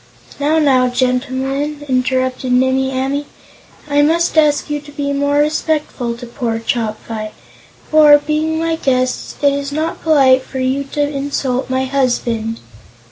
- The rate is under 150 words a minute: Yes, average, 140 wpm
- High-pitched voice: Yes, very high, 275 Hz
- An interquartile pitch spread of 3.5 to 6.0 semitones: No, narrow, 2.4 semitones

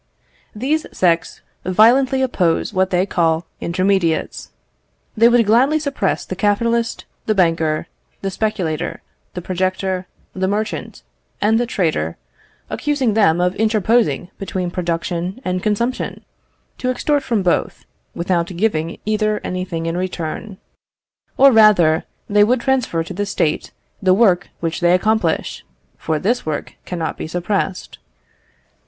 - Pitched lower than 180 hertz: No, high, 190 Hz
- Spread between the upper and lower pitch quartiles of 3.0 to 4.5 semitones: Yes, average, 4.2 semitones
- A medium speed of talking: No, slow, 130 wpm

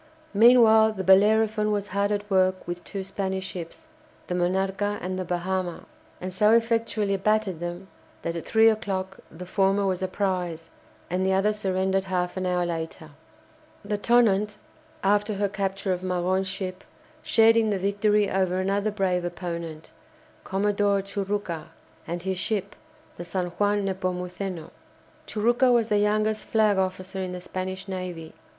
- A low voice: No, high, 190 Hz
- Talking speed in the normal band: Yes, average, 155 wpm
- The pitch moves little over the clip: Yes, narrow, 2.2 semitones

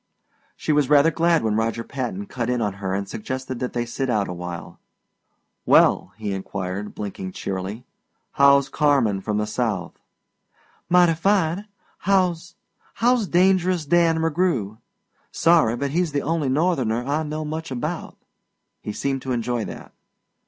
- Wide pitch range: Yes, wide, 7.1 semitones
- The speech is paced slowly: No, average, 150 wpm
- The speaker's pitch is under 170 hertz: Yes, low, 135 Hz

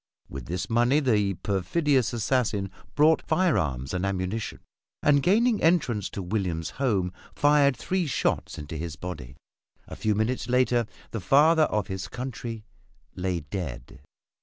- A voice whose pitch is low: Yes, low, 110 Hz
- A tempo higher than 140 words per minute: No, slow, 135 wpm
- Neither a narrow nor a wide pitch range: No, wide, 7.1 semitones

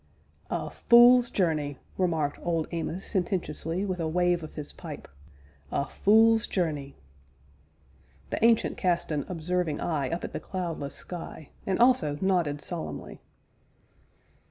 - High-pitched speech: No, medium, 175 Hz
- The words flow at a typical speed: No, slow, 130 wpm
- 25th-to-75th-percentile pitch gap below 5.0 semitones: Yes, average, 3.6 semitones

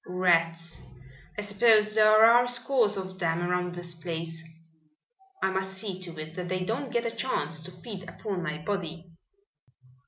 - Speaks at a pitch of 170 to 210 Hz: Yes, medium, 185 Hz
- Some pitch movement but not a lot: Yes, average, 3.9 semitones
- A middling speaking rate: Yes, average, 160 wpm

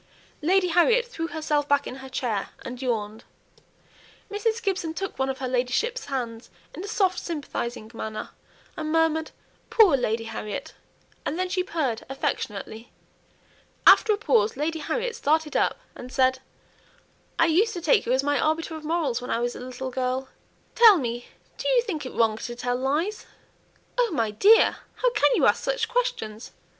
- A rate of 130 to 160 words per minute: No, average, 170 wpm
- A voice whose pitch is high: Yes, very high, 295 Hz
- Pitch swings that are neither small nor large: No, wide, 6.9 semitones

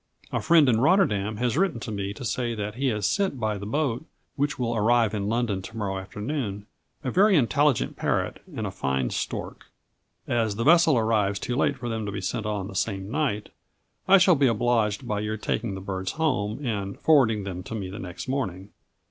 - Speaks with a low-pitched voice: Yes, low, 110 Hz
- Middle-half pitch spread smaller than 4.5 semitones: No, average, 4.8 semitones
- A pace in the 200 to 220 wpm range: Yes, fast, 205 wpm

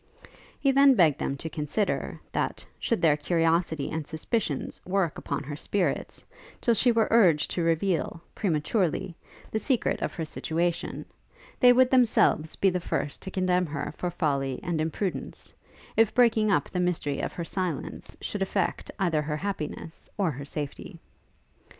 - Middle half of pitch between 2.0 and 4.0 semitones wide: No, average, 4.7 semitones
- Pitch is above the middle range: No, medium, 175 Hz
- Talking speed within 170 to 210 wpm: No, average, 155 wpm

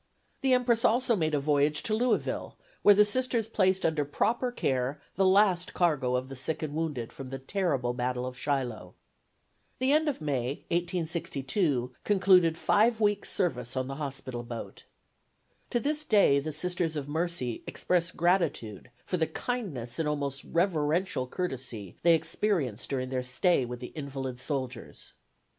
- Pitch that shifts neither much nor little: No, wide, 6.6 semitones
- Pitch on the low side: No, medium, 155 Hz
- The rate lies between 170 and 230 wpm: No, average, 155 wpm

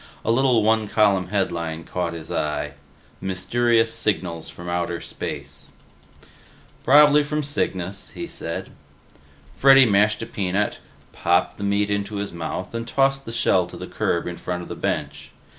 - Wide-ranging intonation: No, average, 4.7 semitones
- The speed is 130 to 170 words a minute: Yes, average, 155 wpm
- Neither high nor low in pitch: No, low, 100 Hz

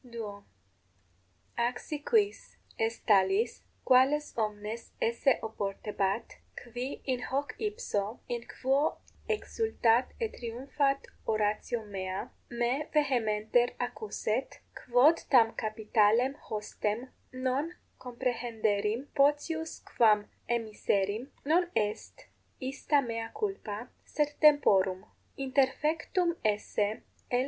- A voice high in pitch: Yes, high, 240 Hz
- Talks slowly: Yes, slow, 100 wpm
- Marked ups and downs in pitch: No, average, 4.6 semitones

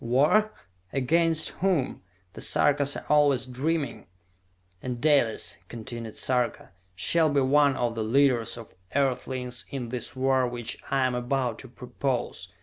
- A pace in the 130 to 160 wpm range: Yes, average, 140 wpm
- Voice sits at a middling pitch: No, low, 130 Hz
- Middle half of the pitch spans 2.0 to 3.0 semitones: Yes, average, 2.7 semitones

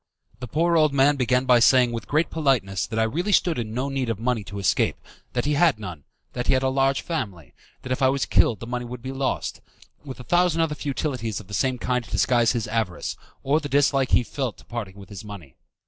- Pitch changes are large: No, average, 3.8 semitones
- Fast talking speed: Yes, fast, 240 wpm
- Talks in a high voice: No, low, 125 Hz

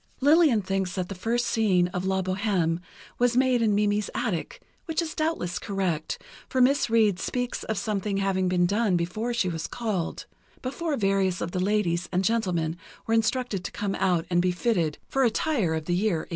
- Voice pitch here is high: Yes, high, 195 Hz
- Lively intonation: No, average, 4.5 semitones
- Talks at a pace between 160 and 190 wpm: Yes, average, 185 wpm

